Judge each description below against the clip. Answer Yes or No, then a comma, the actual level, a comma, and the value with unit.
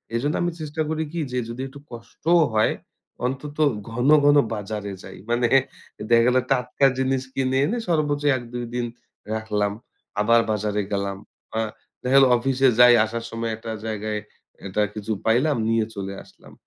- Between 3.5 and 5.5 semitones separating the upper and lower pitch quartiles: Yes, average, 3.8 semitones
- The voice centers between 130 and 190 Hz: No, low, 120 Hz